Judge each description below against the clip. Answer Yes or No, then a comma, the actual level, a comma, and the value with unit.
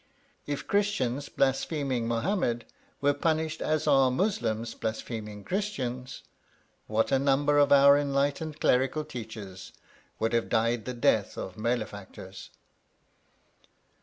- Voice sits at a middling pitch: No, low, 130 Hz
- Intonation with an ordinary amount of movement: Yes, average, 4.1 semitones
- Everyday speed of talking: No, slow, 110 wpm